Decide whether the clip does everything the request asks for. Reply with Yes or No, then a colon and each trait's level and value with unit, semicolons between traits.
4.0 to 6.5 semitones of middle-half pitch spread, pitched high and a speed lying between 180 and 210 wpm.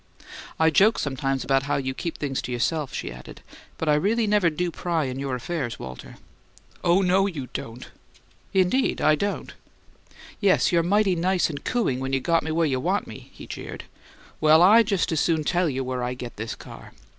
No: wide, 5.4 semitones; medium, 160 Hz; average, 200 wpm